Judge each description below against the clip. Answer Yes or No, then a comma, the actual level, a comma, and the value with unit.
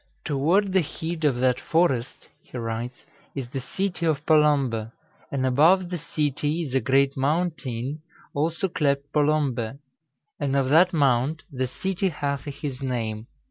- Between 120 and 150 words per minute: Yes, average, 145 wpm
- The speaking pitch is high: No, medium, 140 Hz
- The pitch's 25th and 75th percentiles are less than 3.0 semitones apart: No, average, 3.7 semitones